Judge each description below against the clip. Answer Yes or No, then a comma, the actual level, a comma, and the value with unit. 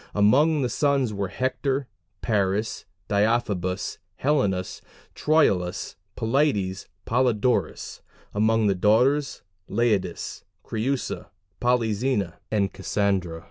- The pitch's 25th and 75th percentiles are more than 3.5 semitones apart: Yes, average, 4.6 semitones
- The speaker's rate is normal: No, slow, 85 wpm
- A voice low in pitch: Yes, low, 110 Hz